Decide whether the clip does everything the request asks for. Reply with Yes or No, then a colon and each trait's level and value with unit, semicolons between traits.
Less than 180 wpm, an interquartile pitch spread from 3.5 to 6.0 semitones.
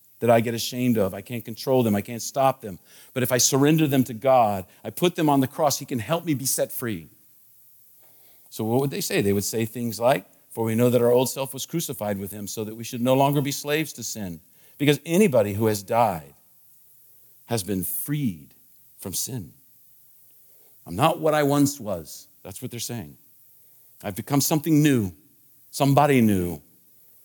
No: average, 200 wpm; average, 4.4 semitones